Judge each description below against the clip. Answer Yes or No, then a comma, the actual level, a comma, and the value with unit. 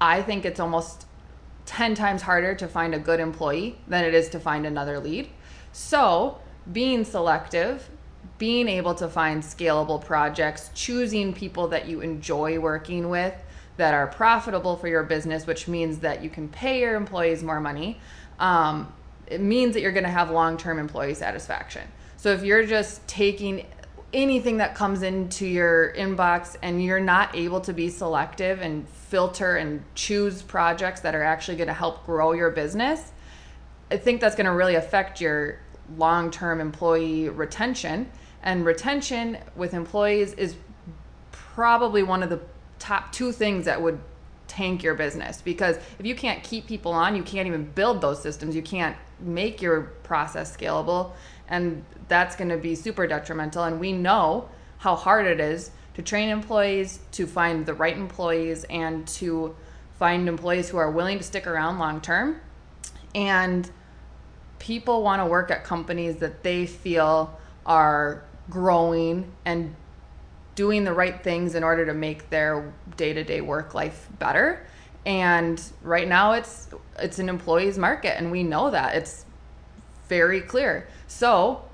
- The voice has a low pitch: No, medium, 170 Hz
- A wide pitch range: No, average, 3.2 semitones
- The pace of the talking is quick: No, average, 160 wpm